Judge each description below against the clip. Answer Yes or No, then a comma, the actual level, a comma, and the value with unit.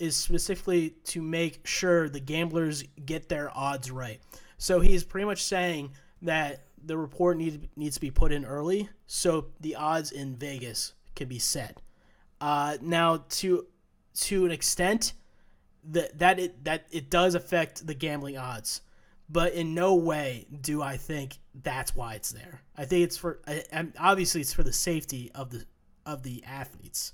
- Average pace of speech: Yes, average, 165 wpm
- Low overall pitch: No, medium, 160 Hz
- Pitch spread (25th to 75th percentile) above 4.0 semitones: No, average, 3.5 semitones